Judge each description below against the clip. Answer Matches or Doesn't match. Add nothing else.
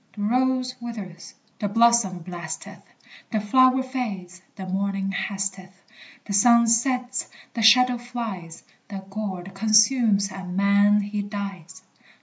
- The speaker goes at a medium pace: Doesn't match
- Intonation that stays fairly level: Doesn't match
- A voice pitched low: Doesn't match